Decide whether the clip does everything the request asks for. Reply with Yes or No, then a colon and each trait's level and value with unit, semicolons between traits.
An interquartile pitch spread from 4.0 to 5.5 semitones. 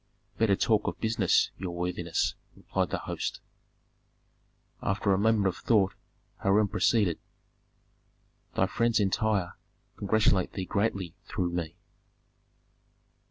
No: average, 3.2 semitones